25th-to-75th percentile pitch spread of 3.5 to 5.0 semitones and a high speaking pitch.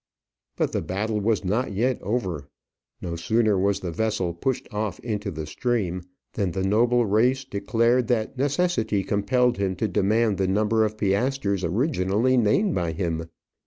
No: average, 4.0 semitones; low, 105 Hz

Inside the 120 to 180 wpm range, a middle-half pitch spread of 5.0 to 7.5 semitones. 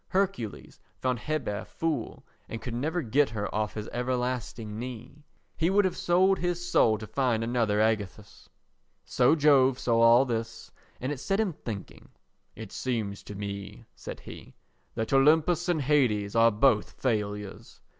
Yes: average, 155 wpm; wide, 5.4 semitones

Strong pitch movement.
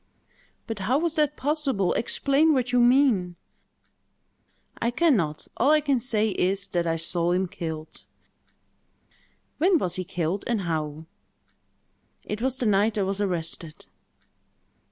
Yes: wide, 7.1 semitones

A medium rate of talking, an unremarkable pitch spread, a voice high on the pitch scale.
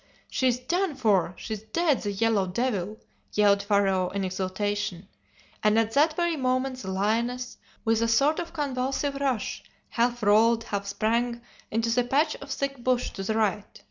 Yes: average, 165 wpm; average, 4.0 semitones; high, 230 Hz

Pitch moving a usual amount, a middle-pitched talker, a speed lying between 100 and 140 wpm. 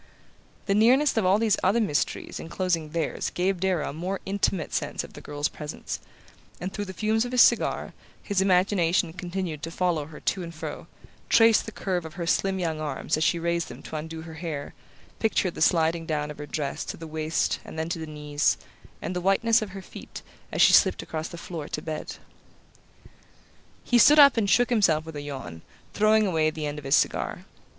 No: average, 4.0 semitones; medium, 170 Hz; fast, 205 wpm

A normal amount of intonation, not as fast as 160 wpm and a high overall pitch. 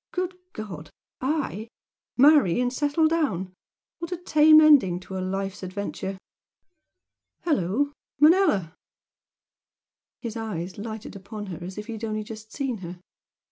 No: wide, 7.5 semitones; slow, 135 wpm; high, 220 Hz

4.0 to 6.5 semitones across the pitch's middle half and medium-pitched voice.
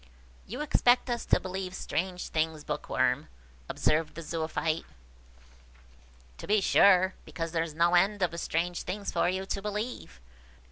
No: average, 3.2 semitones; medium, 180 Hz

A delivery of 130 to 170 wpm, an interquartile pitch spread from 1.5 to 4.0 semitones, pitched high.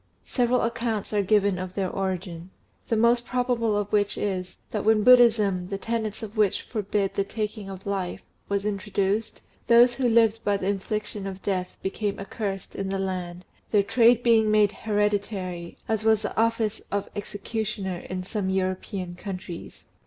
Yes: average, 165 wpm; narrow, 2.5 semitones; high, 205 Hz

